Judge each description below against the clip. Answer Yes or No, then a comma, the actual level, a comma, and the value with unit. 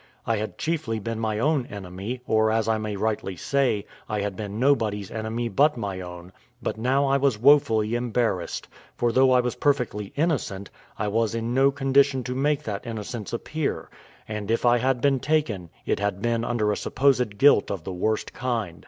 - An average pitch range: Yes, average, 4.1 semitones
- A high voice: No, low, 115 Hz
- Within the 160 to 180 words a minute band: No, average, 190 wpm